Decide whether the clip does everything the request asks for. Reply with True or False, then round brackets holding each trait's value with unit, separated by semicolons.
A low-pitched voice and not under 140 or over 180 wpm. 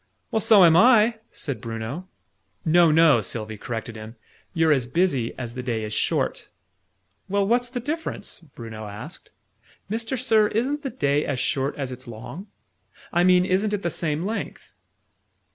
False (165 Hz; 160 wpm)